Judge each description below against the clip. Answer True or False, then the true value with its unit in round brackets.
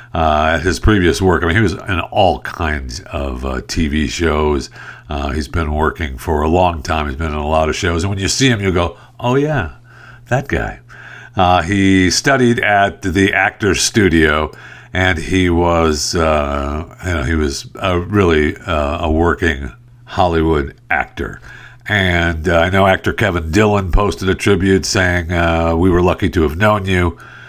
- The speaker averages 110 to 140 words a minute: False (180 wpm)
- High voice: False (90 Hz)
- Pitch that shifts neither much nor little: True (3.9 semitones)